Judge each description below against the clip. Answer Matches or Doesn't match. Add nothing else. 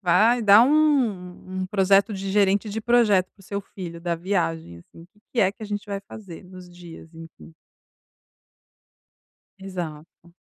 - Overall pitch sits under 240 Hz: Matches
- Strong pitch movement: Doesn't match